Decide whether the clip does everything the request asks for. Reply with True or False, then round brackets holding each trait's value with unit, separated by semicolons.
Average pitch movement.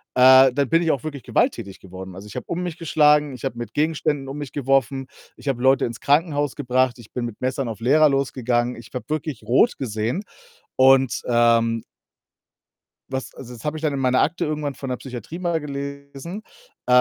True (3.5 semitones)